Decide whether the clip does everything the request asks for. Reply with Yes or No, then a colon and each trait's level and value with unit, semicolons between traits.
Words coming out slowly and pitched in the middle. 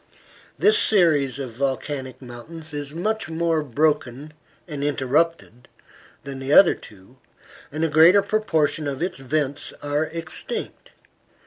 Yes: slow, 125 wpm; medium, 150 Hz